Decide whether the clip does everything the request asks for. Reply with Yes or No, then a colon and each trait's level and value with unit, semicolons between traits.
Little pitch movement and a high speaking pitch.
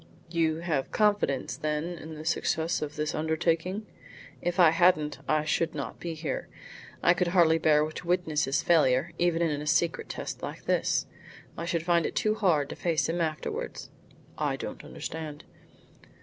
No: narrow, 2.1 semitones; medium, 160 Hz